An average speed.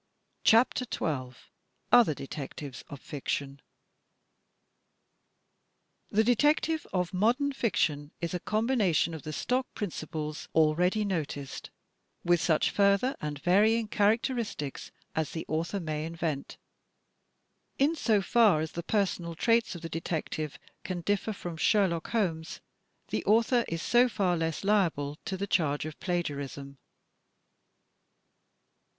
No: slow, 120 wpm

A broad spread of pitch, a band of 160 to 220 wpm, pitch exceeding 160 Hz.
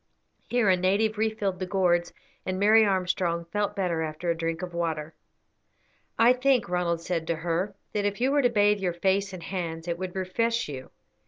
No: average, 3.4 semitones; average, 190 wpm; medium, 185 Hz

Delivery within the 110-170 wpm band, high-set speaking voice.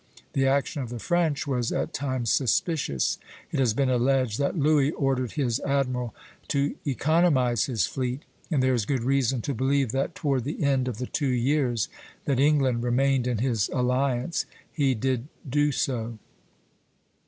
No: average, 165 wpm; low, 130 Hz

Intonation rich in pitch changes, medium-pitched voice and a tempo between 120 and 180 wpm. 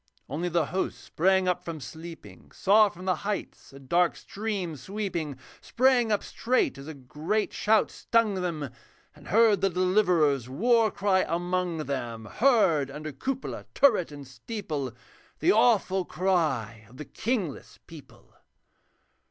Yes: wide, 5.8 semitones; medium, 180 Hz; average, 140 wpm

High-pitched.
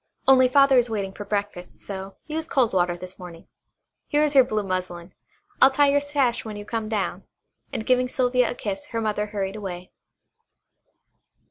Yes: high, 215 Hz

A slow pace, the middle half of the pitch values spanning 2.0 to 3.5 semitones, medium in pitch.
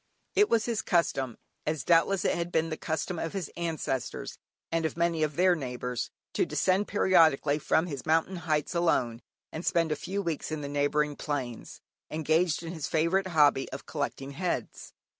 No: average, 180 wpm; average, 3.1 semitones; medium, 160 Hz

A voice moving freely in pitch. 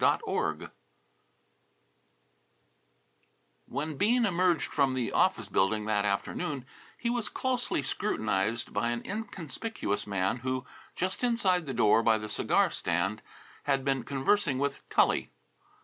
Yes: wide, 9.0 semitones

